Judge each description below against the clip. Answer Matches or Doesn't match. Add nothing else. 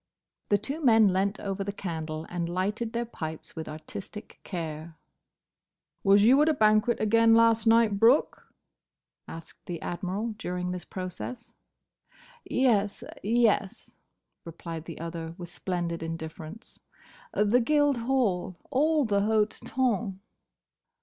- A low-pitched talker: Doesn't match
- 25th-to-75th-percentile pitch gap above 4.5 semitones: Matches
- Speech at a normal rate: Doesn't match